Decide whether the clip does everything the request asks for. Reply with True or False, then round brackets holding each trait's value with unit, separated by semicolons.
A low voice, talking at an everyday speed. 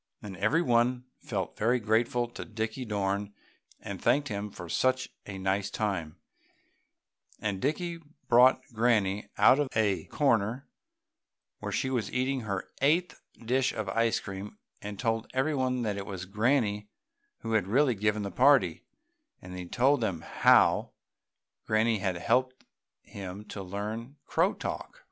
True (110 Hz; 145 wpm)